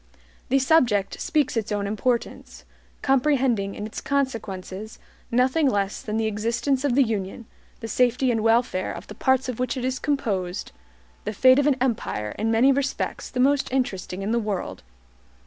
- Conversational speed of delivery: Yes, average, 170 wpm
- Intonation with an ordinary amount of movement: Yes, average, 4.0 semitones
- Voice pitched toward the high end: Yes, high, 235 Hz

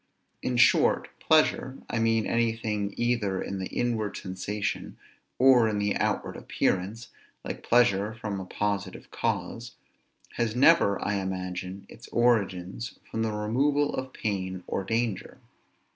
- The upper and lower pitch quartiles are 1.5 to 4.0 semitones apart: Yes, average, 3.3 semitones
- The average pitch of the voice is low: Yes, low, 110 Hz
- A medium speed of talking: No, slow, 130 wpm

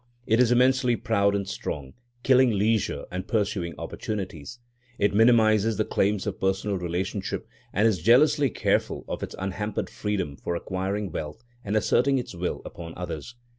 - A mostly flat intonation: No, average, 3.5 semitones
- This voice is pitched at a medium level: No, low, 105 Hz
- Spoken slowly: No, average, 155 wpm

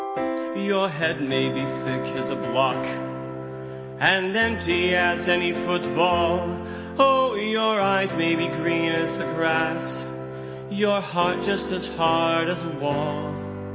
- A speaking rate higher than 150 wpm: No, average, 140 wpm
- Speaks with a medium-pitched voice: Yes, medium, 165 Hz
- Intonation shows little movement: No, average, 4.6 semitones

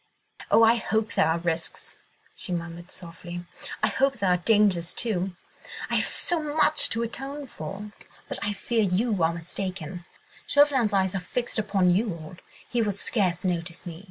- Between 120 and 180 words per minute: Yes, average, 165 wpm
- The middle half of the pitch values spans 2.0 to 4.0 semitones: No, average, 4.6 semitones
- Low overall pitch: No, high, 195 Hz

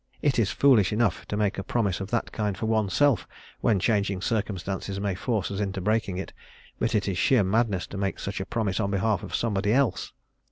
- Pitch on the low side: Yes, low, 100 Hz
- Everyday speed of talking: No, fast, 210 wpm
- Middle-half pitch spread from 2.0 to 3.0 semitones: Yes, narrow, 2.6 semitones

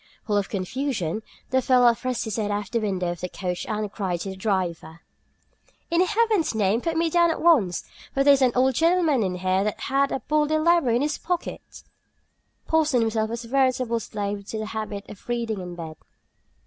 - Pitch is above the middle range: Yes, high, 230 Hz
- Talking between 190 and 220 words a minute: Yes, fast, 205 wpm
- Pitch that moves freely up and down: Yes, wide, 5.7 semitones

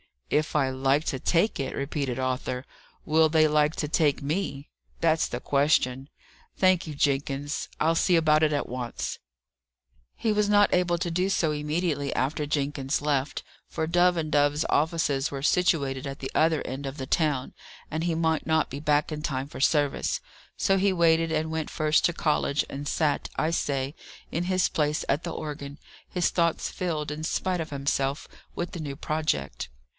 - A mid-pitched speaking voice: Yes, medium, 150 Hz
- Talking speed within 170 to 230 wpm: Yes, average, 180 wpm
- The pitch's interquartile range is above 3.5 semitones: No, average, 2.9 semitones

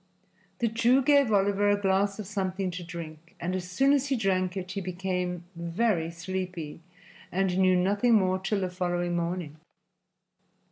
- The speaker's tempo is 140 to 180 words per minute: Yes, average, 160 wpm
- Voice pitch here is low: No, medium, 185 Hz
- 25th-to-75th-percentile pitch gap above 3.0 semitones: No, narrow, 2.4 semitones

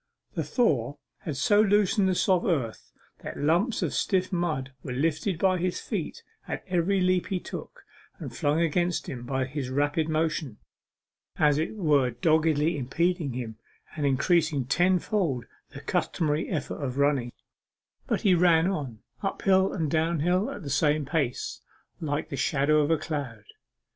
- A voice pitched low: No, medium, 155 Hz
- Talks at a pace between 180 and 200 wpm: No, average, 155 wpm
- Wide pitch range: No, average, 4.2 semitones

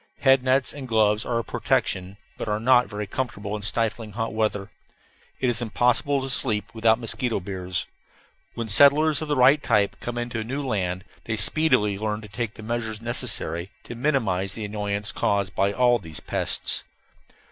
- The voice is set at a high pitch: No, low, 110 Hz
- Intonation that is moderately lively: Yes, average, 3.2 semitones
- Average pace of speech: Yes, average, 180 wpm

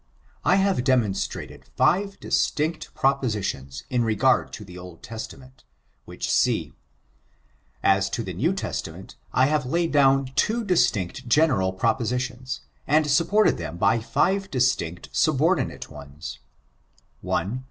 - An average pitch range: No, wide, 8.0 semitones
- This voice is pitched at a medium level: No, low, 130 Hz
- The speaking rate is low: Yes, slow, 125 wpm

